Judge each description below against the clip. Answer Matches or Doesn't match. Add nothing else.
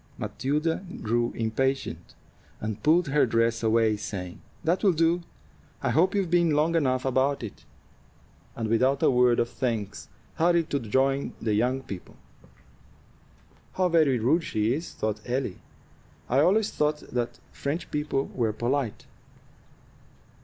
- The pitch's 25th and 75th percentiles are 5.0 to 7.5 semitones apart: Matches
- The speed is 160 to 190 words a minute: Doesn't match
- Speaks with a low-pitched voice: Matches